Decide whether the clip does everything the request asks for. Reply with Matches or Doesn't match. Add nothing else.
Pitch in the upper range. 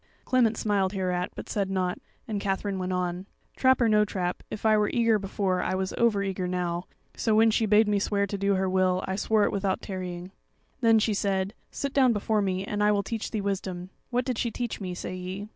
Matches